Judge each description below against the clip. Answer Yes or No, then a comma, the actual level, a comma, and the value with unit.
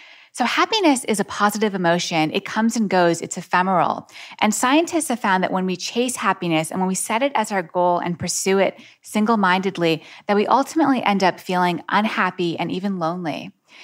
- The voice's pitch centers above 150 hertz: Yes, high, 190 Hz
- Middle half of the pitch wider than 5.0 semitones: No, average, 3.8 semitones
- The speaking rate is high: No, average, 185 wpm